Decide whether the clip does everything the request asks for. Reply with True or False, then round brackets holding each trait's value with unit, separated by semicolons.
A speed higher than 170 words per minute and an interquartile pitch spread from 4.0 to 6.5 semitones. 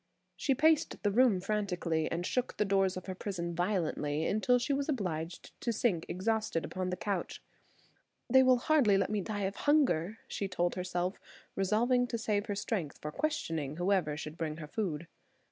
True (180 wpm; 4.7 semitones)